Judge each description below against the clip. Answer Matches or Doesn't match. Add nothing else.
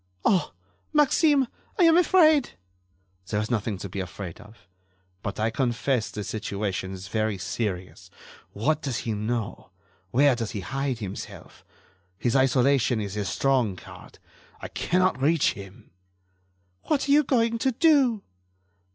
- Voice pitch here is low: Matches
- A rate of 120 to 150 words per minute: Matches